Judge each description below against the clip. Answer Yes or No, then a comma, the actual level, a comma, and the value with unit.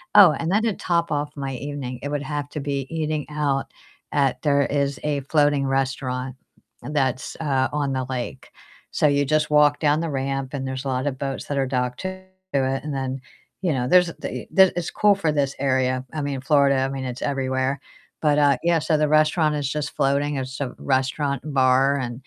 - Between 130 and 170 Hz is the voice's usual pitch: Yes, medium, 140 Hz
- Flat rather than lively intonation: Yes, narrow, 2.2 semitones